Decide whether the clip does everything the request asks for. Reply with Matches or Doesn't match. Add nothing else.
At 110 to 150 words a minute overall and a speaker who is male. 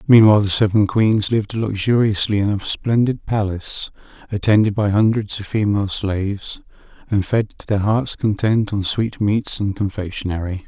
Matches